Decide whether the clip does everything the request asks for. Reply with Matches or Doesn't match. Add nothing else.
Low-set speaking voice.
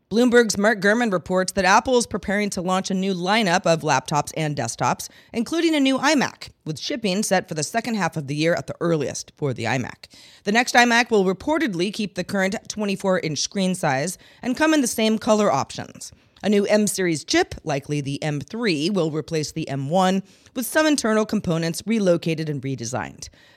Doesn't match